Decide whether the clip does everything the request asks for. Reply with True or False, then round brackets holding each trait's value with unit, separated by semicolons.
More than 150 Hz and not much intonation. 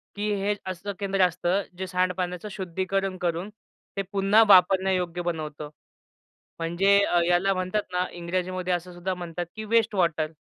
True (185 Hz; 1.9 semitones)